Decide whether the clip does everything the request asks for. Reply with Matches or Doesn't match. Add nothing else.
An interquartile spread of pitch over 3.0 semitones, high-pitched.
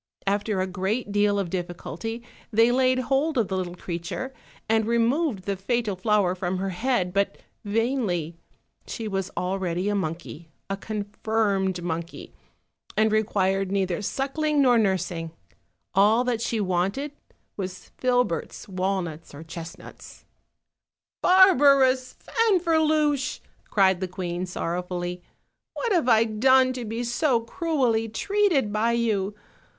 Matches